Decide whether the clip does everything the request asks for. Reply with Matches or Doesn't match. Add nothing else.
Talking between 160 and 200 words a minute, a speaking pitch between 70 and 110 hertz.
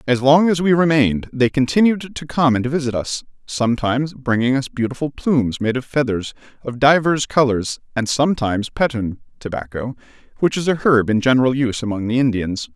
Doesn't match